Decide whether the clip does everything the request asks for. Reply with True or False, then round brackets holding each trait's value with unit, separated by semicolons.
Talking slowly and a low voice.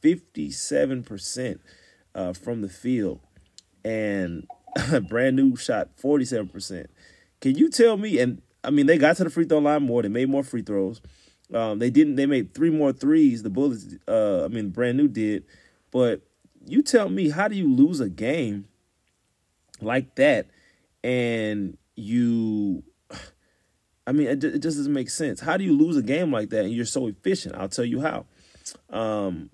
False (175 wpm; 125 Hz)